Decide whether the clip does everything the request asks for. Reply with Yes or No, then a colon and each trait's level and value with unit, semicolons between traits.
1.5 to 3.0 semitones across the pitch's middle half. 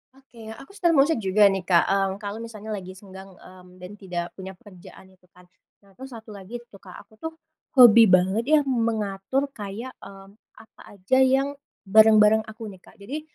No: average, 3.5 semitones